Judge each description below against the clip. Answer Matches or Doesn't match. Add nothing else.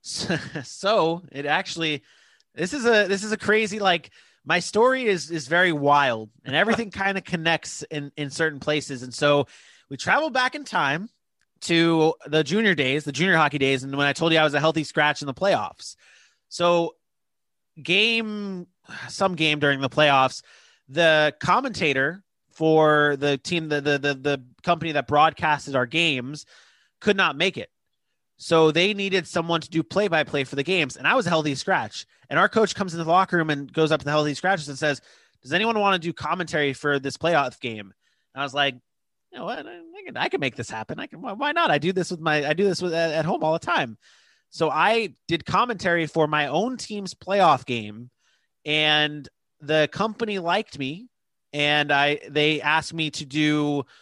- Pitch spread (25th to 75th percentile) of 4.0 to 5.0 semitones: Matches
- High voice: Doesn't match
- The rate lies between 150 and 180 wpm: Doesn't match